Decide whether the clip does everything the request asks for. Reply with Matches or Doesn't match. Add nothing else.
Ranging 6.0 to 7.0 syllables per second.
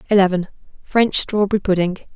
Matches